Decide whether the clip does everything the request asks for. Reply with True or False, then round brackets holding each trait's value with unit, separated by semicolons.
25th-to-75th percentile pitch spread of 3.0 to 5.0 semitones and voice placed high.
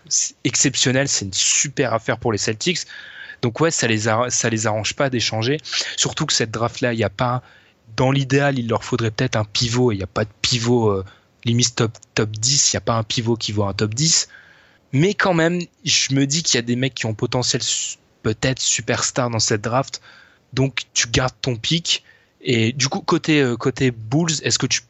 False (3.5 semitones; 125 Hz)